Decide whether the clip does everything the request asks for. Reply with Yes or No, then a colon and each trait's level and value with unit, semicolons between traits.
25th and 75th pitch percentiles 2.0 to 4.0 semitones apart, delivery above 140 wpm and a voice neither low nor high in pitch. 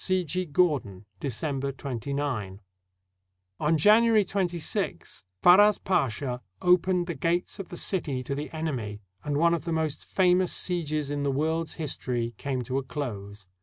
No: average, 5.1 semitones; average, 155 wpm; medium, 150 Hz